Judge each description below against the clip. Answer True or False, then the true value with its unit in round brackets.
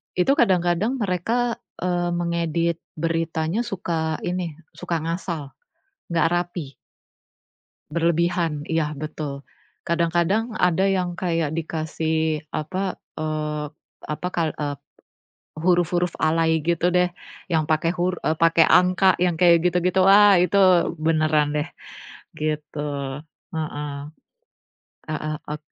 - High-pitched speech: False (170 Hz)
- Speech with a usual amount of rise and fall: False (2.3 semitones)